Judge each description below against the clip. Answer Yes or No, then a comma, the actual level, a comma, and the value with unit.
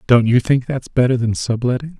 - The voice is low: Yes, low, 120 Hz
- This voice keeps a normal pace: No, fast, 210 wpm